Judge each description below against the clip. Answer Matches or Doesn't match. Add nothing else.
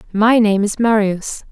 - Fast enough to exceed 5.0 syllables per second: Doesn't match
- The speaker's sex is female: Matches